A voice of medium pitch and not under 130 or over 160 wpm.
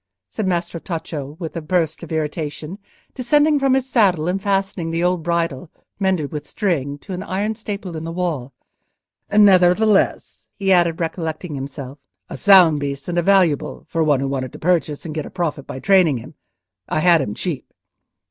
No: medium, 170 Hz; average, 180 wpm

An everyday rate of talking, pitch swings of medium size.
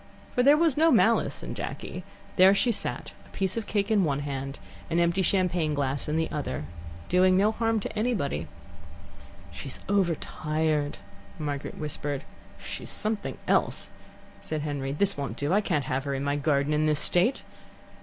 No: average, 170 wpm; wide, 5.7 semitones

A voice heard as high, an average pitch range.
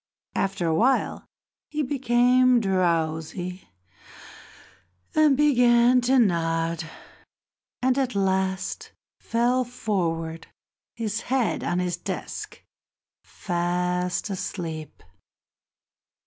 No: high, 195 Hz; wide, 6.1 semitones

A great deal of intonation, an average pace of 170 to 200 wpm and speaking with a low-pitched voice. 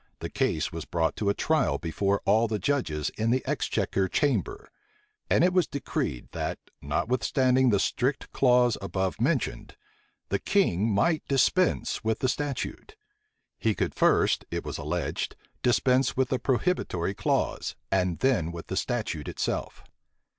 No: wide, 6.0 semitones; average, 145 wpm; low, 120 Hz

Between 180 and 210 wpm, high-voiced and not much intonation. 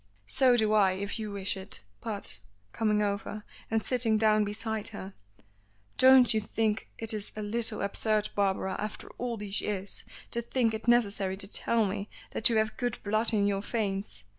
Yes: average, 185 wpm; high, 215 Hz; narrow, 1.9 semitones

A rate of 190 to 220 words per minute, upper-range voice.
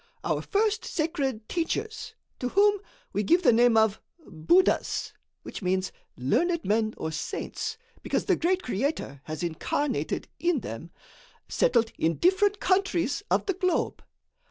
No: slow, 135 wpm; very high, 290 Hz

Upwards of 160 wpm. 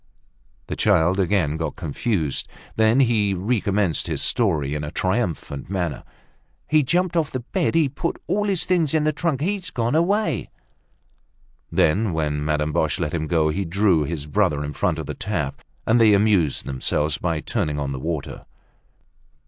Yes: average, 170 wpm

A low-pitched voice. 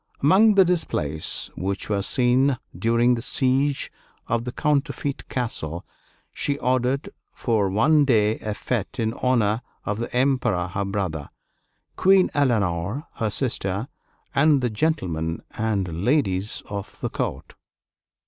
Yes: low, 120 Hz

